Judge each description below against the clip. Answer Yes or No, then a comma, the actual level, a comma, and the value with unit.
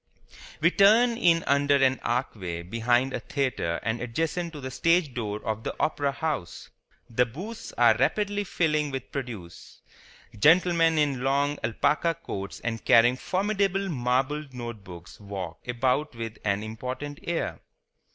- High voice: No, low, 135 Hz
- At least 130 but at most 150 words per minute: Yes, average, 140 wpm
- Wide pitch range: Yes, wide, 6.1 semitones